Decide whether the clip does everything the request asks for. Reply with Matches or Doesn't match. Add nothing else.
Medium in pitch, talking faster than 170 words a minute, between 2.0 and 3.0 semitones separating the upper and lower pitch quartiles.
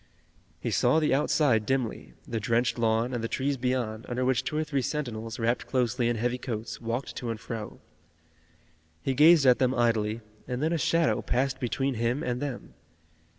Doesn't match